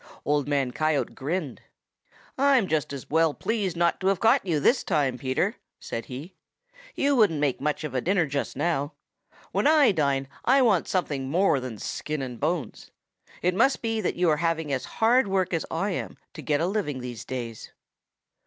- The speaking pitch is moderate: Yes, medium, 160 Hz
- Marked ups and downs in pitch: Yes, wide, 5.9 semitones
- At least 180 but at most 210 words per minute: Yes, average, 190 wpm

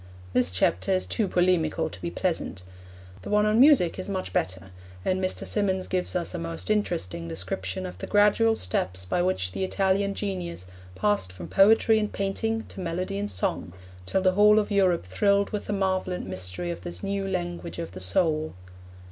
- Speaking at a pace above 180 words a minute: Yes, average, 190 wpm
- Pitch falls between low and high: Yes, medium, 180 Hz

